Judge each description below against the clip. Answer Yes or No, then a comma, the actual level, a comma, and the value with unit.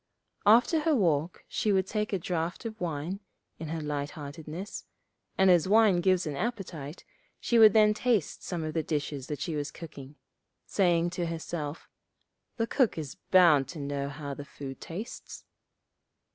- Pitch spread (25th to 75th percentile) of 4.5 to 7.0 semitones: Yes, average, 5.1 semitones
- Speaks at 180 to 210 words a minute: No, average, 165 wpm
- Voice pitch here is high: No, medium, 170 Hz